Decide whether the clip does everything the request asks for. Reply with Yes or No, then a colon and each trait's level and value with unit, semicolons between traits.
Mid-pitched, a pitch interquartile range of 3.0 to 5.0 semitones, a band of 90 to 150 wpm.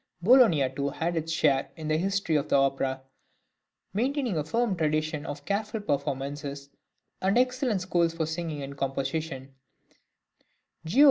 No: medium, 160 Hz; wide, 5.6 semitones; average, 140 wpm